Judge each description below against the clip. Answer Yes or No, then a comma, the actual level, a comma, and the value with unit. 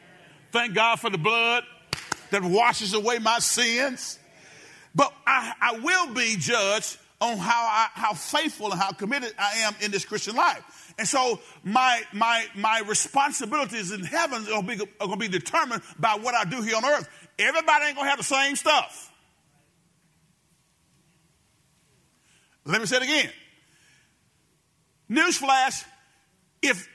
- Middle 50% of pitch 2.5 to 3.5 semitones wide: No, average, 4.1 semitones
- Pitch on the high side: Yes, high, 225 Hz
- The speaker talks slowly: No, average, 145 wpm